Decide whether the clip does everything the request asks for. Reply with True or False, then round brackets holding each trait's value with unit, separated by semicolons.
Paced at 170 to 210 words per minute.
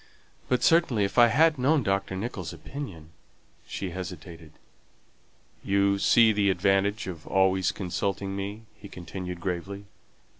False (135 wpm)